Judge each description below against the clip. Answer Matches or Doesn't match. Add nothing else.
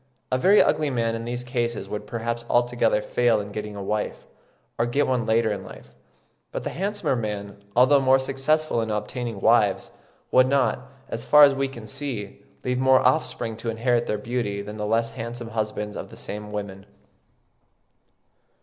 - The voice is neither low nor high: Doesn't match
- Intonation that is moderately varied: Matches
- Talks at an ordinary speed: Matches